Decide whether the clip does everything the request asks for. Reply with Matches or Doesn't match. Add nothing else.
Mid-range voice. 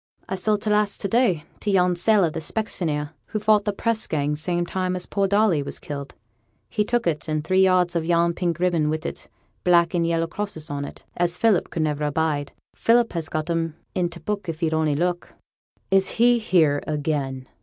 Matches